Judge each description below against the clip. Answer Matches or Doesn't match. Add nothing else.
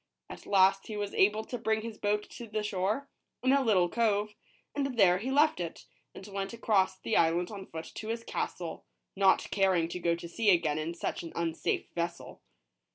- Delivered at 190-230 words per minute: Matches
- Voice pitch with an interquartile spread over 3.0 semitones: Matches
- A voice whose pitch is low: Doesn't match